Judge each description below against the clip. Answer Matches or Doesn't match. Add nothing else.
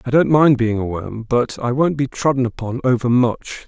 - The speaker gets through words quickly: Matches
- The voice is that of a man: Matches